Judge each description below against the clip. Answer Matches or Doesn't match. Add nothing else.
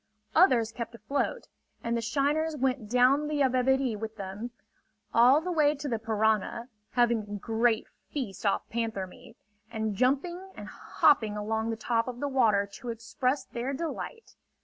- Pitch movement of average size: Matches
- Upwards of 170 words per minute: Doesn't match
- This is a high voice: Matches